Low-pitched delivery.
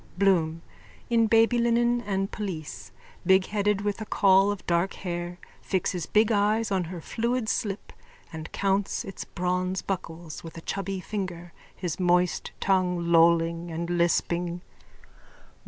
No: medium, 185 Hz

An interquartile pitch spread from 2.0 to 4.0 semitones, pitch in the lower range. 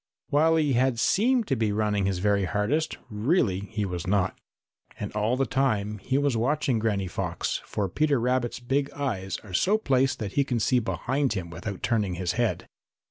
No: average, 5.2 semitones; low, 115 Hz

